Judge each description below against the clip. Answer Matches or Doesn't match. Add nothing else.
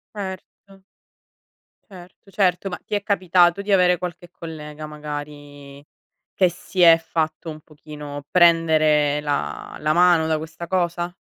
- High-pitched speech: Doesn't match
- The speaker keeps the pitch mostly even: Doesn't match